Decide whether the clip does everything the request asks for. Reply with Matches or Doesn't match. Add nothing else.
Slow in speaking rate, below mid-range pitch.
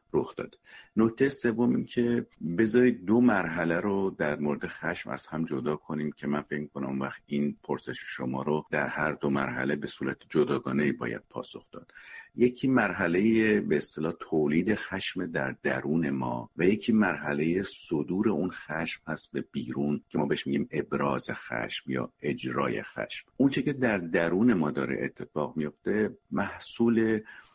Doesn't match